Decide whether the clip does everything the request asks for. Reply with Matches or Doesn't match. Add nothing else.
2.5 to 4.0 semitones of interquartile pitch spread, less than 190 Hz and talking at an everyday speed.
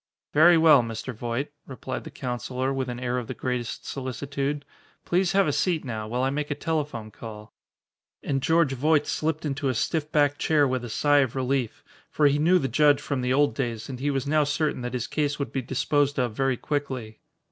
Doesn't match